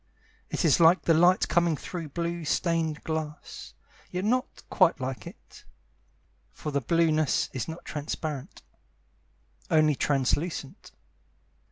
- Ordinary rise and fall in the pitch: No, narrow, 2.3 semitones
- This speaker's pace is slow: Yes, slow, 120 wpm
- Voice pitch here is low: No, medium, 160 Hz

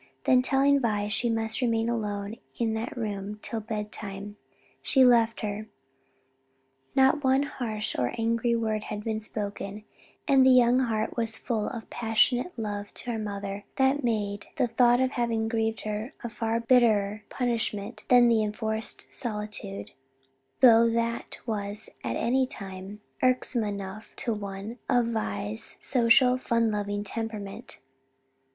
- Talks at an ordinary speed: Yes, average, 145 wpm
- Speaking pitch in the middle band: No, high, 225 Hz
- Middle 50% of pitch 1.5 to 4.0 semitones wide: Yes, narrow, 2.5 semitones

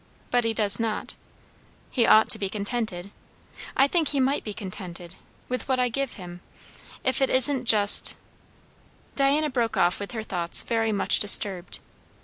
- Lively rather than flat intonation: No, average, 4.5 semitones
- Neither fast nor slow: Yes, average, 160 wpm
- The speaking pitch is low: No, high, 225 Hz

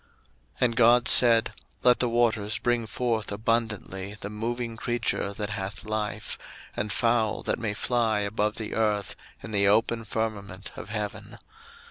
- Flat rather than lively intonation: Yes, narrow, 2.2 semitones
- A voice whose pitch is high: No, low, 110 Hz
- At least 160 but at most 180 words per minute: No, average, 150 wpm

